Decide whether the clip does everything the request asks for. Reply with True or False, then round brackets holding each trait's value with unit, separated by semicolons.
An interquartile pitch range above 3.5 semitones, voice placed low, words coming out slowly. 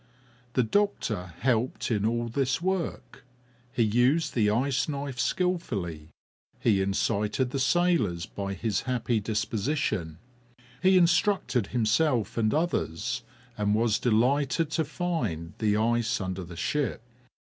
True (5.4 semitones; 120 Hz; 125 wpm)